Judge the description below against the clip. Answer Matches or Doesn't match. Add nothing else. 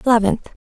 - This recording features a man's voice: Doesn't match